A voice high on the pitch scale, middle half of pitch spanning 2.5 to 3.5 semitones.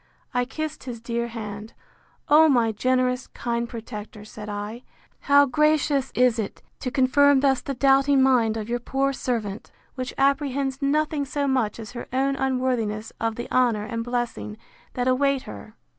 Yes: very high, 250 Hz; average, 3.2 semitones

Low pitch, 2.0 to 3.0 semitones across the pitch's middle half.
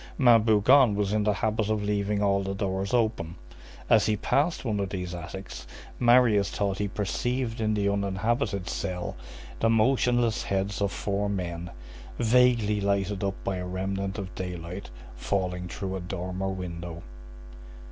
Yes: low, 100 Hz; narrow, 2.5 semitones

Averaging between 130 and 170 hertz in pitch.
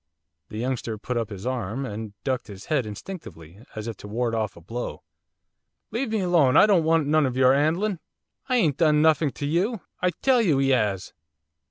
Yes: low, 135 Hz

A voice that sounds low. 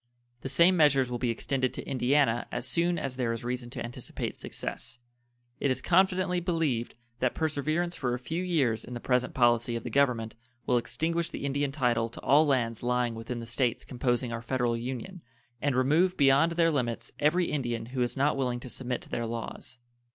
Yes: low, 130 Hz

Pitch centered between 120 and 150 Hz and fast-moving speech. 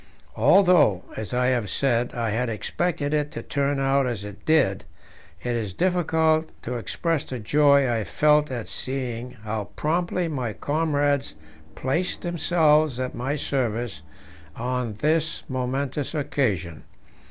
No: low, 135 Hz; slow, 135 wpm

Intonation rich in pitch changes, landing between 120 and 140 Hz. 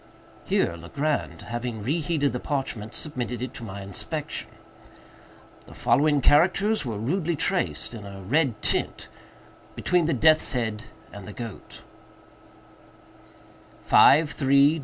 Yes: wide, 5.8 semitones; low, 135 Hz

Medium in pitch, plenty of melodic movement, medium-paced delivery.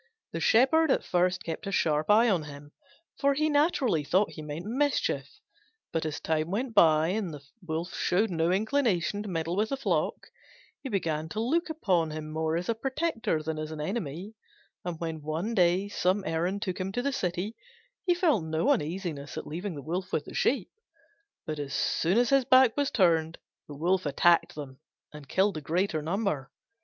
Yes: medium, 180 Hz; wide, 5.8 semitones; average, 190 wpm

